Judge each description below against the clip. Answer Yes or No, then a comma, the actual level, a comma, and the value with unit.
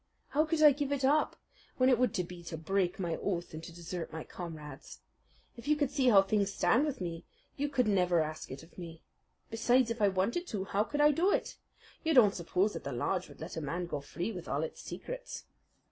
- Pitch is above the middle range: Yes, high, 195 Hz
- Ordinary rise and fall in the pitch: No, wide, 7.7 semitones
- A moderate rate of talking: No, fast, 230 wpm